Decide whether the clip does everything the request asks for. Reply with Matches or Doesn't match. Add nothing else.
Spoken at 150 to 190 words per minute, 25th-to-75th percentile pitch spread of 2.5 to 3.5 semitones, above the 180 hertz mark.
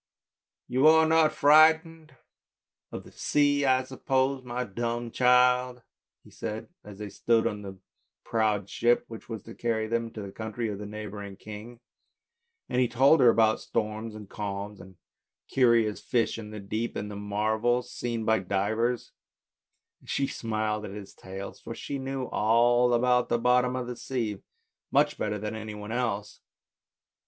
Doesn't match